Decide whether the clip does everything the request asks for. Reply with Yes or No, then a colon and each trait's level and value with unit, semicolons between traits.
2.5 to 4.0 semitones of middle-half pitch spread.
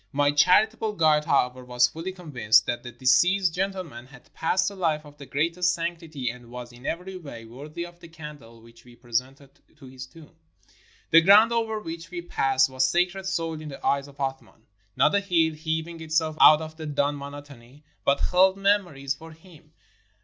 No: average, 4.7 semitones